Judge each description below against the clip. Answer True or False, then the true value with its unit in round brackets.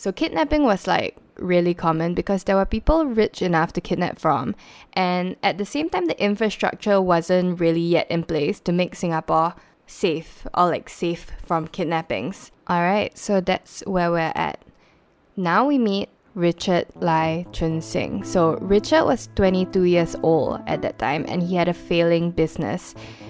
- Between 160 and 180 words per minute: True (165 wpm)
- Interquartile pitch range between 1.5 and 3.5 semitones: True (2.9 semitones)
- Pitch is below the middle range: False (180 Hz)